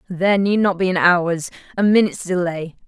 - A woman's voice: Yes, female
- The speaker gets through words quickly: No, average, 190 wpm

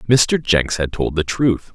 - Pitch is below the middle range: Yes, low, 100 Hz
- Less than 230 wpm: Yes, fast, 205 wpm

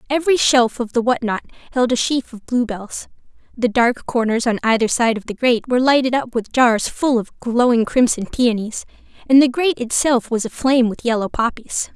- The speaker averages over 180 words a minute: Yes, average, 195 wpm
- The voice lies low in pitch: No, high, 240 Hz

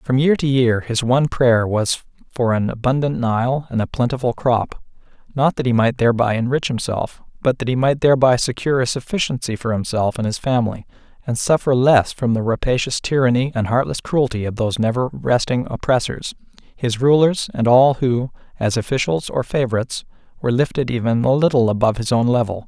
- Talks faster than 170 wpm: Yes, average, 185 wpm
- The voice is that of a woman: No, male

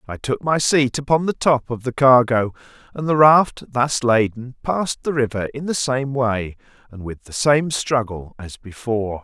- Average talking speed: Yes, average, 190 wpm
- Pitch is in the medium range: No, low, 125 Hz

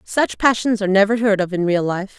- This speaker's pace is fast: Yes, fast, 245 wpm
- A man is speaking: No, female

